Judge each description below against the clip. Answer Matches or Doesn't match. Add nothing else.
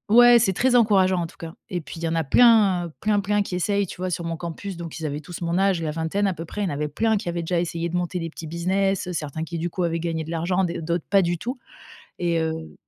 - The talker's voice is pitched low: Doesn't match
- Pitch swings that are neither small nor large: Matches